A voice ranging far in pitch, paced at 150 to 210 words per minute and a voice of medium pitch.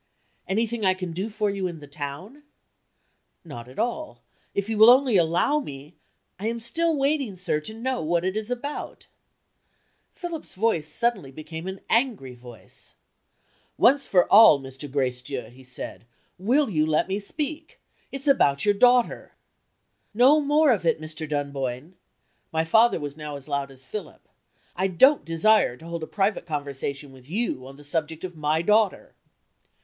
Yes: wide, 7.9 semitones; average, 170 wpm; medium, 180 Hz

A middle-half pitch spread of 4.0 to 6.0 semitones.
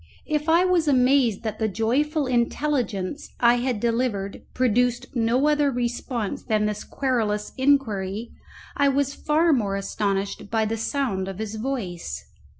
Yes: average, 4.8 semitones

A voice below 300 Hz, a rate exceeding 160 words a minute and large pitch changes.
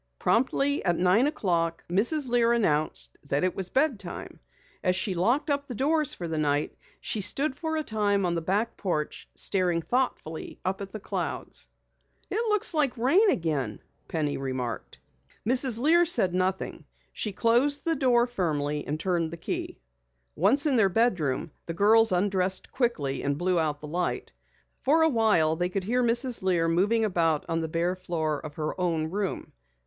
Yes: high, 190 Hz; average, 170 wpm; wide, 6.6 semitones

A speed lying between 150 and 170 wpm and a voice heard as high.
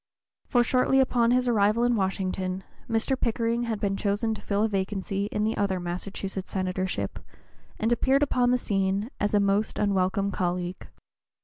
Yes: average, 165 wpm; high, 205 Hz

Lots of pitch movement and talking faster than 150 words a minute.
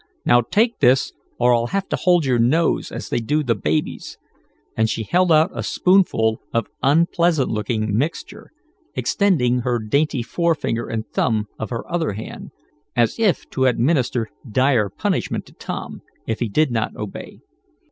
Yes: wide, 6.3 semitones; average, 160 wpm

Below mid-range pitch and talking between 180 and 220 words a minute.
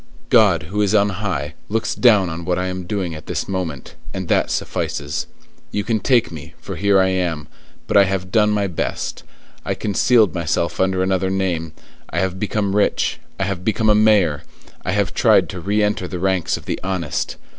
Yes: very low, 95 Hz; average, 200 wpm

